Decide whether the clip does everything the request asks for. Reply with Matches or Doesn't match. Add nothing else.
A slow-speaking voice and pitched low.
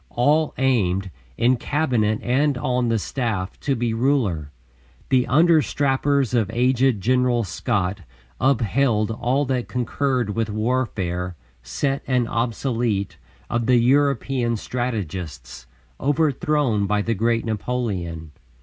Matches